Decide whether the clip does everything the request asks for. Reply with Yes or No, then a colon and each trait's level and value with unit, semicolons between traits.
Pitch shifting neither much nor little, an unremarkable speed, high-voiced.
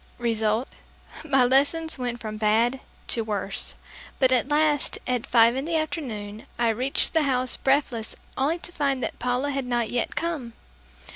Yes: average, 3.6 semitones; average, 160 wpm; very high, 250 Hz